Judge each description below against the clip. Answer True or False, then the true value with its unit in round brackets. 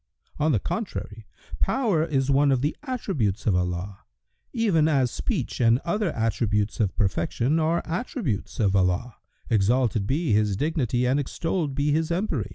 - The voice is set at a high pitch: False (130 Hz)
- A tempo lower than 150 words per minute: False (155 wpm)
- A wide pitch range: True (7.4 semitones)